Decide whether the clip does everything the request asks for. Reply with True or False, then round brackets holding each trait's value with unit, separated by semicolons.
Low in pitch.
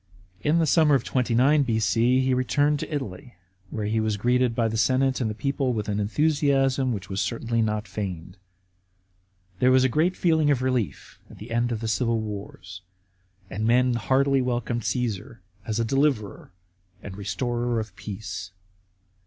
True (120 Hz)